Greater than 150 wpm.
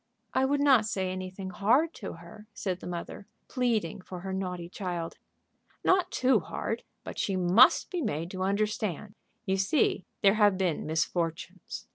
Yes: average, 160 wpm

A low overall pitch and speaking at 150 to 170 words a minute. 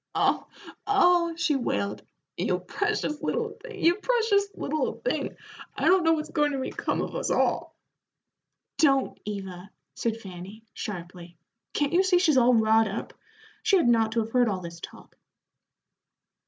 No: very high, 265 Hz; average, 155 wpm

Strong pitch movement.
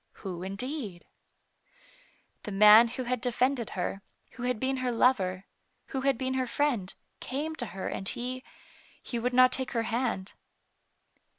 No: average, 3.7 semitones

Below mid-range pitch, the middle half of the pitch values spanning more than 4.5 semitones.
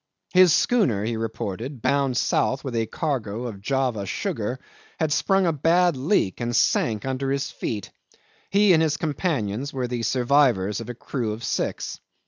Yes: low, 130 Hz; average, 4.9 semitones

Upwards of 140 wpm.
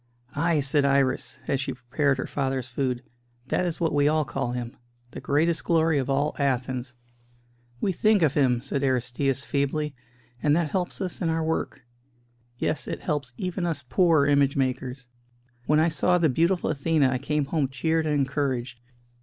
Yes: average, 175 wpm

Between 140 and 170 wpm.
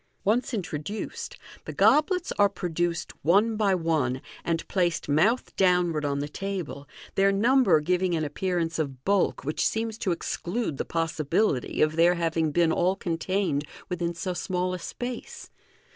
Yes: average, 155 wpm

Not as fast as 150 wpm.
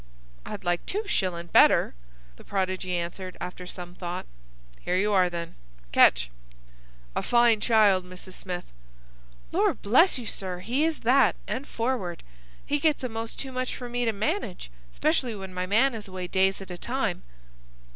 No: average, 160 wpm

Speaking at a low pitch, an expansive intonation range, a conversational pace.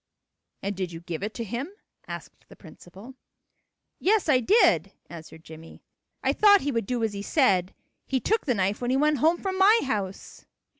No: high, 235 Hz; wide, 8.2 semitones; average, 190 wpm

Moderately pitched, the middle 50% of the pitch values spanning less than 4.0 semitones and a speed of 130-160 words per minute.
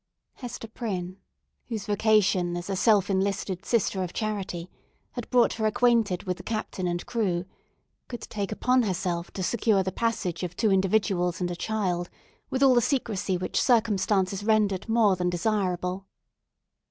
No: high, 200 Hz; average, 3.4 semitones; average, 150 wpm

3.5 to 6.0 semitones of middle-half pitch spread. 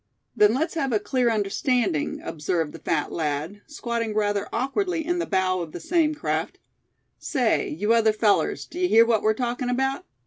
Yes: average, 5.0 semitones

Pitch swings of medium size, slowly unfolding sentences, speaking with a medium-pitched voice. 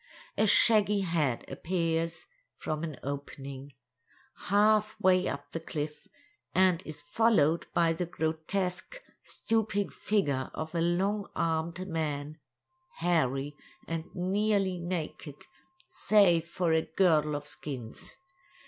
Yes: average, 4.0 semitones; slow, 110 wpm; medium, 165 Hz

